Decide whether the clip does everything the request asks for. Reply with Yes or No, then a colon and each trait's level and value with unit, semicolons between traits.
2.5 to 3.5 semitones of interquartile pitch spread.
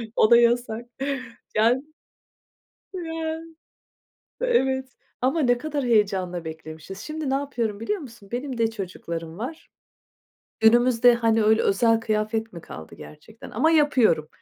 No: average, 4.0 semitones